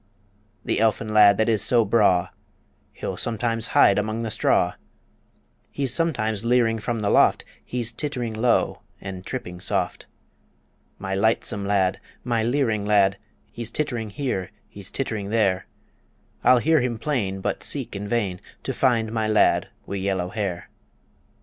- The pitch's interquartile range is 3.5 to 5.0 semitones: No, average, 3.0 semitones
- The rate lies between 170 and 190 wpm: No, average, 145 wpm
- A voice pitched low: Yes, low, 110 Hz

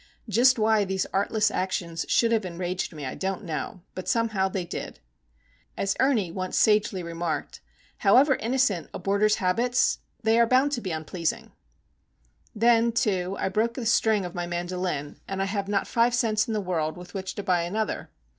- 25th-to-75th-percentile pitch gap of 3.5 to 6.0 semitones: Yes, average, 3.8 semitones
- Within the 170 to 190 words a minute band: Yes, average, 175 wpm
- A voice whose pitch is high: Yes, high, 195 Hz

